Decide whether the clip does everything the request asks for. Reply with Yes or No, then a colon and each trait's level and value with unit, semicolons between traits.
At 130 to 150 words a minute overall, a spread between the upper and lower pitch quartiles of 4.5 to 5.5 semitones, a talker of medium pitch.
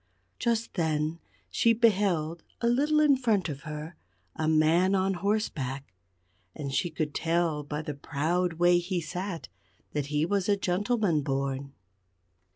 Yes: average, 145 wpm; average, 4.8 semitones; medium, 170 Hz